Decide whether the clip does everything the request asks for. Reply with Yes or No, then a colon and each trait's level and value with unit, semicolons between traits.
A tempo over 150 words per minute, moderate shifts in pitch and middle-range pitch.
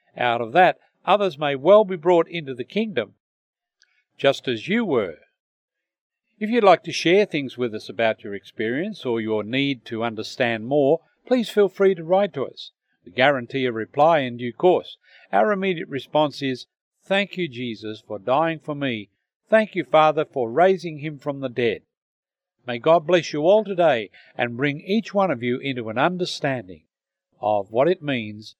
No: average, 180 wpm; wide, 7.0 semitones; medium, 150 Hz